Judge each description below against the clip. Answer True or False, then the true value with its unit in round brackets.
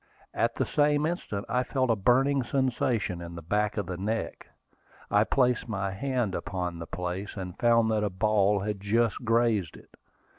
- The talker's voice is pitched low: True (105 Hz)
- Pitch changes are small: False (4.0 semitones)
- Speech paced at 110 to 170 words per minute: False (180 wpm)